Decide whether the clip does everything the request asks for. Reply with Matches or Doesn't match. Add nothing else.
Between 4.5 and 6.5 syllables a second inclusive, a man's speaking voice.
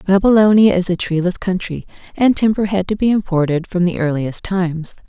Doesn't match